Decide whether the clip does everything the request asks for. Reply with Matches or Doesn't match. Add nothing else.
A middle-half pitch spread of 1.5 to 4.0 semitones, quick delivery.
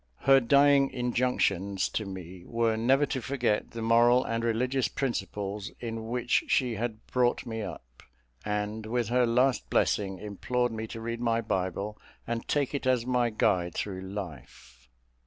Doesn't match